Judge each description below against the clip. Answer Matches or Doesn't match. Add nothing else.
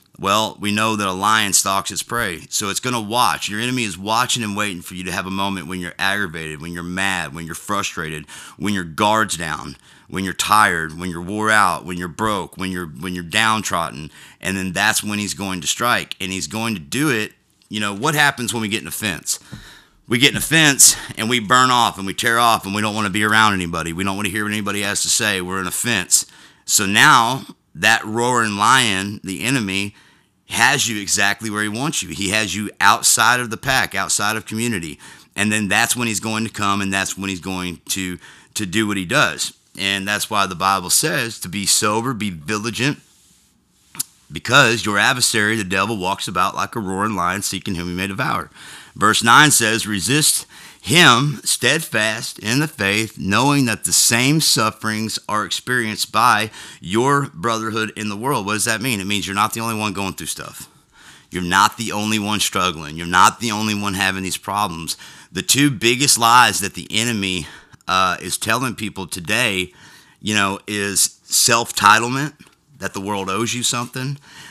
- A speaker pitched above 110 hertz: Doesn't match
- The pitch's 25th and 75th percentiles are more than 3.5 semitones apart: Doesn't match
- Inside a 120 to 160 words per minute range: Doesn't match